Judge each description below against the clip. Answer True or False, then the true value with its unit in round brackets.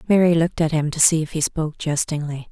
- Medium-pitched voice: True (160 Hz)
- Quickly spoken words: True (240 wpm)